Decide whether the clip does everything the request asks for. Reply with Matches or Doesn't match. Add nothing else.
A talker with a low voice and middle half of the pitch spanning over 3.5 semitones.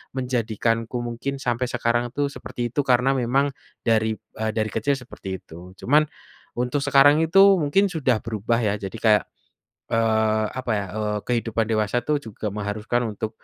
Doesn't match